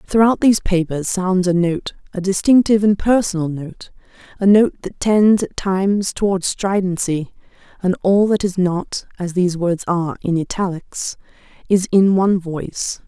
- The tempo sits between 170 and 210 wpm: No, average, 155 wpm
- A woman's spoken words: Yes, female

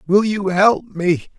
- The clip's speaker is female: No, male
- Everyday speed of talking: Yes, average, 175 wpm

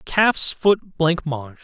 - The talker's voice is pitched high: No, medium, 165 Hz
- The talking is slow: Yes, slow, 110 wpm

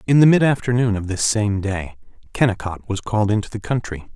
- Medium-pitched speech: No, low, 105 Hz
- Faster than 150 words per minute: Yes, average, 200 wpm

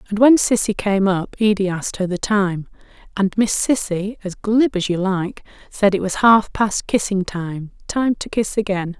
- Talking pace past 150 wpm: Yes, average, 195 wpm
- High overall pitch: Yes, high, 200 Hz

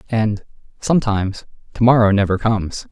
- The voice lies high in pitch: No, low, 110 Hz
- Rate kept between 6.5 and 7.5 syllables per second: No, 5.7 syllables/s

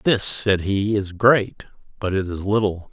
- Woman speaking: No, male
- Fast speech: No, average, 185 wpm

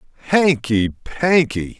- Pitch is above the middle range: No, low, 135 Hz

